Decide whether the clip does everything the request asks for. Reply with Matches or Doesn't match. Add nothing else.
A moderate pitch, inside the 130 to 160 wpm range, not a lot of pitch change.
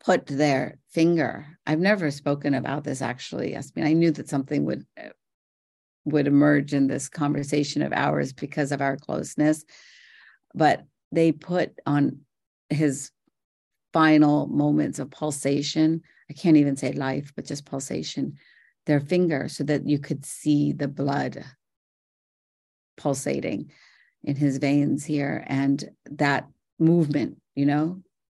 Matches